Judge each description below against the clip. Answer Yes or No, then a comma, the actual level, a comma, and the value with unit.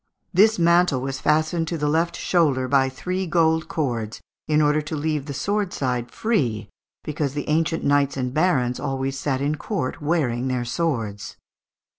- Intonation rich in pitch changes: No, average, 4.0 semitones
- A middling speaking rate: Yes, average, 165 wpm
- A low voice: No, medium, 145 Hz